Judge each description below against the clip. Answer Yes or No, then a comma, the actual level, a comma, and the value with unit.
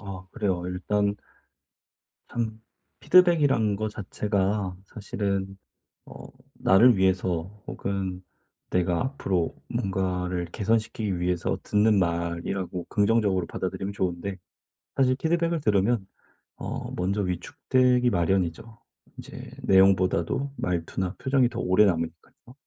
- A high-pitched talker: No, very low, 95 Hz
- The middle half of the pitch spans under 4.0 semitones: Yes, average, 3.3 semitones